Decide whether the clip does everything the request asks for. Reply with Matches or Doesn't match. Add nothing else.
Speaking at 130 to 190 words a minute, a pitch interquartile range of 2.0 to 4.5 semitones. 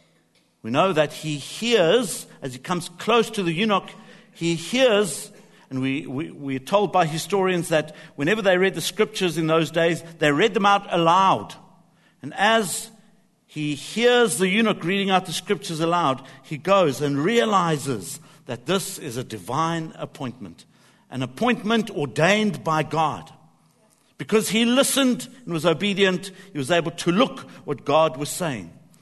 Doesn't match